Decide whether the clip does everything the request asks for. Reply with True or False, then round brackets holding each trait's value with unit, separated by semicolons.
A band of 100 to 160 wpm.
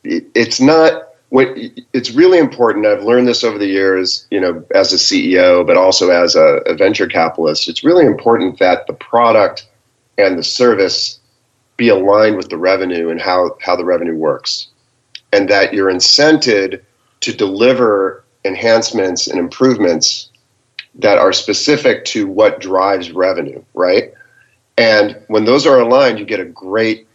True (155 wpm)